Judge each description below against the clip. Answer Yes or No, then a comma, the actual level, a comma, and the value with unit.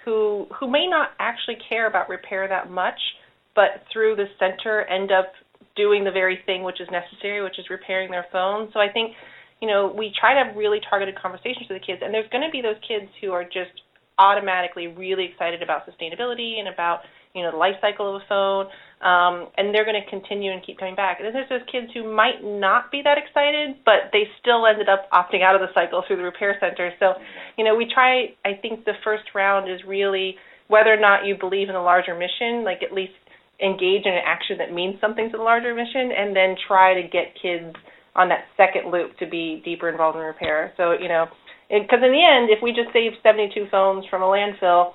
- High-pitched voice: Yes, high, 195 Hz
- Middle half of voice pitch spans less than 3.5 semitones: Yes, average, 2.9 semitones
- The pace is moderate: No, fast, 225 wpm